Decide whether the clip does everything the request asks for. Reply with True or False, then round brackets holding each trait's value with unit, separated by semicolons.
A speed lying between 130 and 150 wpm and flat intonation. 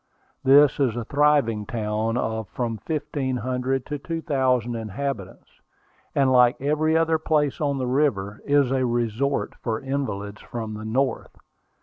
False (145 wpm; 4.0 semitones)